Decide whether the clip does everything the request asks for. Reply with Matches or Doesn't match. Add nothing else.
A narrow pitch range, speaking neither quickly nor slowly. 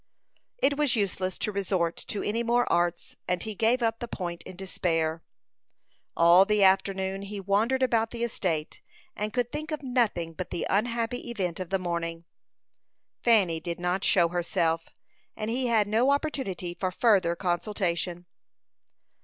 Doesn't match